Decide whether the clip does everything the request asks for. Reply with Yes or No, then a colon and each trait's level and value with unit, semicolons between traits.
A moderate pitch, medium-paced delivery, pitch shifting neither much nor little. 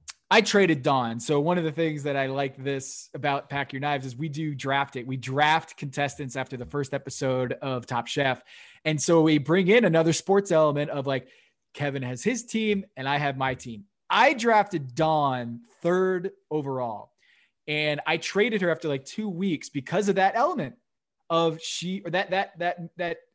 Yes: medium, 150 Hz; average, 195 wpm; average, 4.5 semitones